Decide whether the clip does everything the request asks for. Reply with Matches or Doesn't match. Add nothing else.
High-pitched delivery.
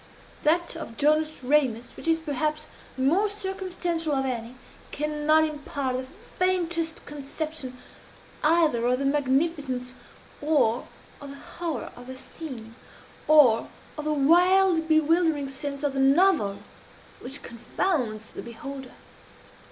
Matches